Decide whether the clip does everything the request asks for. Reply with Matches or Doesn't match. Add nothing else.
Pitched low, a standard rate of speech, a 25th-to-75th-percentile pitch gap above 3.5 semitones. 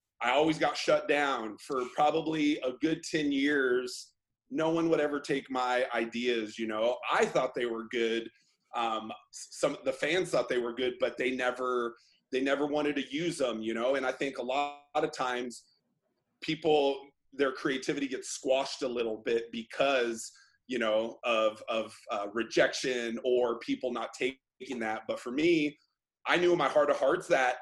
Matches